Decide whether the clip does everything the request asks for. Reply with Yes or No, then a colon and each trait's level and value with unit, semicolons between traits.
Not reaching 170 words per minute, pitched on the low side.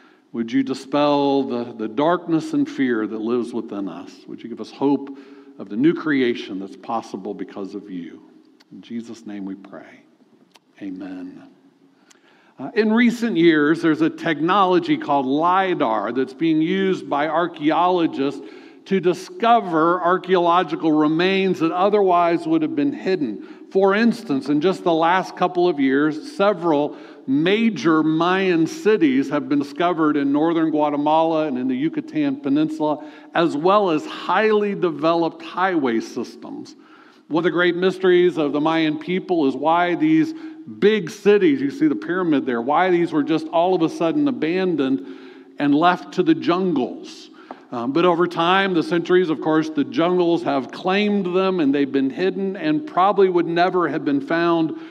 No: average, 155 wpm; medium, 175 Hz